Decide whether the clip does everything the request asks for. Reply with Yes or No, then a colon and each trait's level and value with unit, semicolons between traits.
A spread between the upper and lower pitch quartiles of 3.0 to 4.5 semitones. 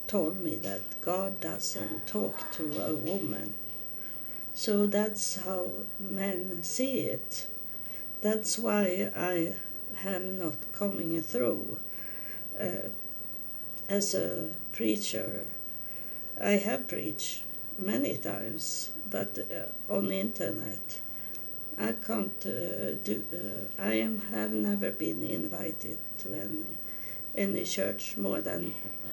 Yes: average, 3.3 semitones